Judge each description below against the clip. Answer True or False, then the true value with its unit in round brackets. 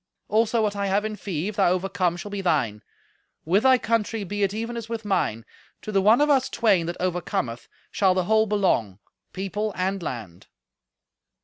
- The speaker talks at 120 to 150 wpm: False (190 wpm)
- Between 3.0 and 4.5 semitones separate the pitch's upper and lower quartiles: True (3.5 semitones)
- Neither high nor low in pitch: False (200 Hz)